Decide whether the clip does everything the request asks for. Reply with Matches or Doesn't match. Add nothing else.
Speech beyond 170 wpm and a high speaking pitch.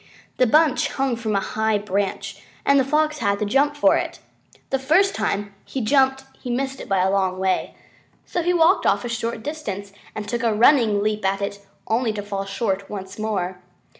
Matches